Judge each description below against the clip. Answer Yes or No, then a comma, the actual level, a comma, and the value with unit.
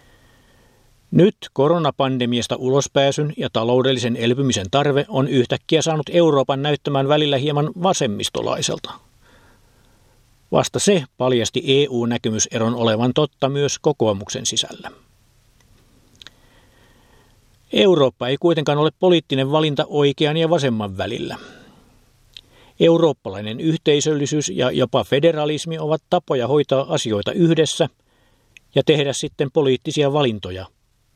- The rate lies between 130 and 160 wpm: No, slow, 95 wpm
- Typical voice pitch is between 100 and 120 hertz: No, low, 130 Hz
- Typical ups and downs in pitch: Yes, average, 4.0 semitones